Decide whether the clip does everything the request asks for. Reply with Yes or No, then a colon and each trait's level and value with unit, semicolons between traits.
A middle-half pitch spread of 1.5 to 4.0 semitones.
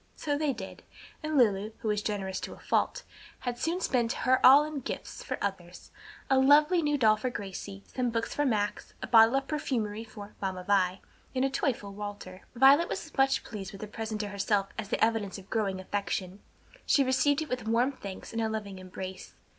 No: average, 5.0 semitones